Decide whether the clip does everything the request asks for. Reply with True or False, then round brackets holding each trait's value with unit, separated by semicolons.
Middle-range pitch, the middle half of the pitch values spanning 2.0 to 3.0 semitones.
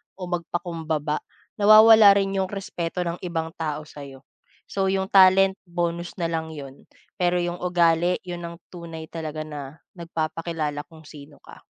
True (170 Hz; 2.6 semitones)